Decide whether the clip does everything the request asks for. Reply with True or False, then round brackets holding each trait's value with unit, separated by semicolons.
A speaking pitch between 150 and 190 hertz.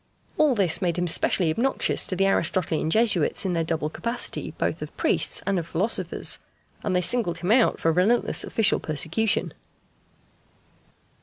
True (185 Hz)